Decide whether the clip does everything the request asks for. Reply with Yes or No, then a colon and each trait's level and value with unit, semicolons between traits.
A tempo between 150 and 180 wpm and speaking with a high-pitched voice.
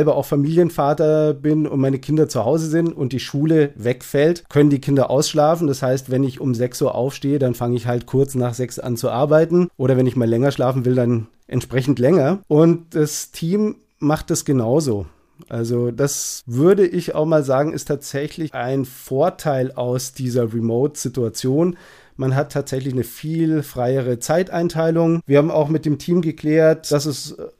No: average, 175 wpm; medium, 140 Hz